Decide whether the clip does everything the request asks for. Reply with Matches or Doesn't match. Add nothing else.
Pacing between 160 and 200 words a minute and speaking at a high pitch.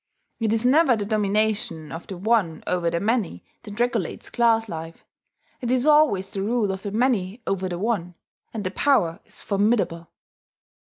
Matches